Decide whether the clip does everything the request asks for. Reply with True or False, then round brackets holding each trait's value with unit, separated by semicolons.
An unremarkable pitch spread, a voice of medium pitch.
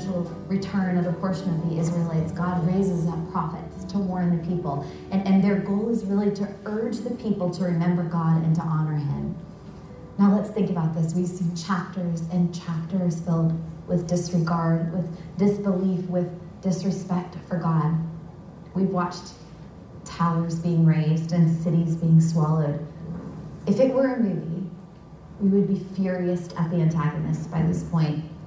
False (2.2 semitones; 175 Hz)